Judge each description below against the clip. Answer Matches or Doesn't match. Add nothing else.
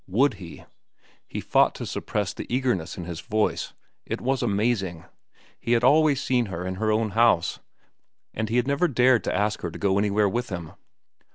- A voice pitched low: Matches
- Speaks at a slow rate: Doesn't match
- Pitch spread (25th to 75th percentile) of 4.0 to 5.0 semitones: Matches